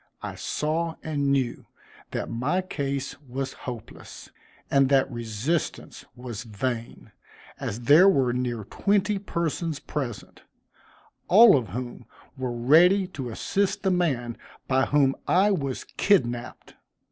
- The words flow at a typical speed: No, slow, 125 wpm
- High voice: No, low, 135 Hz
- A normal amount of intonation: No, wide, 5.7 semitones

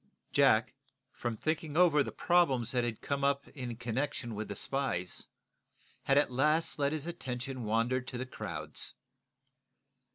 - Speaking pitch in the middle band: No, low, 130 Hz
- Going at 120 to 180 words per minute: Yes, average, 150 wpm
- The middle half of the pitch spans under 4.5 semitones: Yes, average, 3.4 semitones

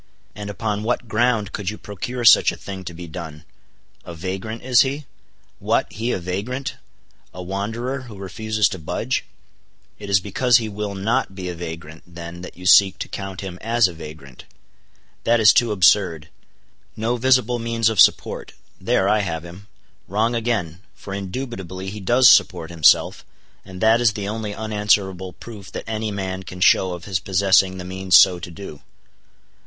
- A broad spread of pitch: No, average, 3.5 semitones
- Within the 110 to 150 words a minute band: No, average, 175 wpm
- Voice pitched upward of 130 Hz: No, low, 100 Hz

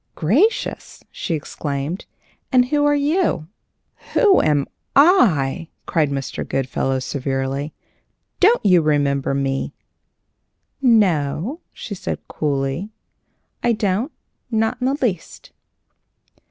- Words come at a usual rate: No, slow, 100 wpm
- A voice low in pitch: No, medium, 165 Hz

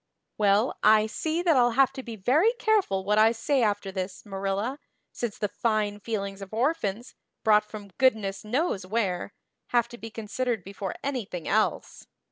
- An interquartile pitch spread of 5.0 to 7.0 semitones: No, average, 3.8 semitones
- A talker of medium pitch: No, high, 215 Hz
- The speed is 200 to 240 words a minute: No, average, 165 wpm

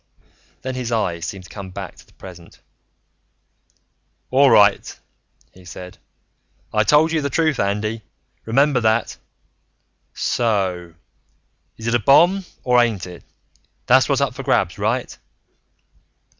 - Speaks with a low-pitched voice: Yes, low, 110 Hz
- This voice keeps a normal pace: No, slow, 130 wpm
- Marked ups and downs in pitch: Yes, wide, 5.7 semitones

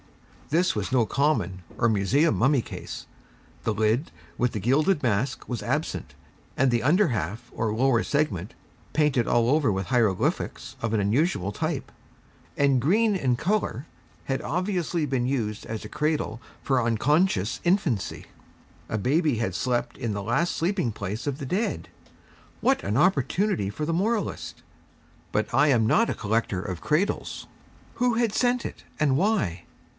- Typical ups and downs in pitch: No, wide, 6.6 semitones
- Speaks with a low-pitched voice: Yes, low, 130 Hz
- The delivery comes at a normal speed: Yes, average, 155 wpm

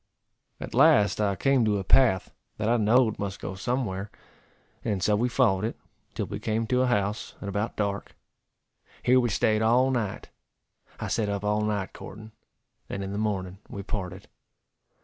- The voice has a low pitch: Yes, low, 105 Hz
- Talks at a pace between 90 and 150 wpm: No, average, 175 wpm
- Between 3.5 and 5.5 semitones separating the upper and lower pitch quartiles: No, average, 2.7 semitones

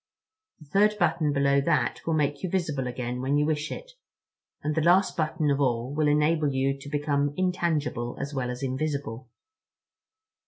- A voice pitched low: No, medium, 145 Hz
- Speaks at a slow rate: No, average, 170 wpm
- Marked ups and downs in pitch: No, narrow, 2.6 semitones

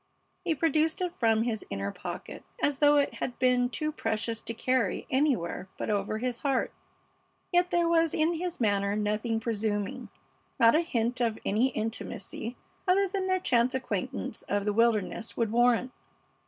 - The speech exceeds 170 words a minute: No, average, 165 wpm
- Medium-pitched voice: No, high, 240 Hz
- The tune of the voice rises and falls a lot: Yes, wide, 5.8 semitones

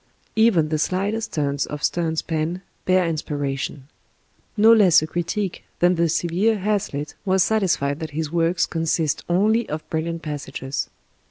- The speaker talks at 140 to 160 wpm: Yes, average, 145 wpm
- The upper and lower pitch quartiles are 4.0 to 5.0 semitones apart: No, average, 3.6 semitones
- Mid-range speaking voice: Yes, medium, 165 Hz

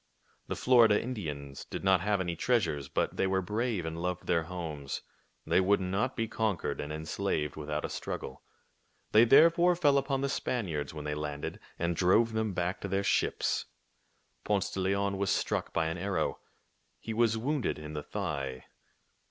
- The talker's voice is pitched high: No, very low, 95 Hz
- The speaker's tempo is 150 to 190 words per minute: Yes, average, 175 wpm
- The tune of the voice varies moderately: No, wide, 6.0 semitones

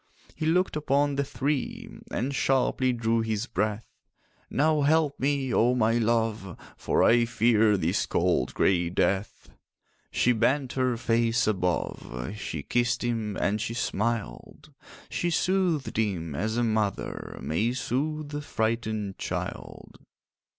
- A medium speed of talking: No, slow, 130 wpm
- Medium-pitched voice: No, low, 115 Hz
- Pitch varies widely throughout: No, average, 4.0 semitones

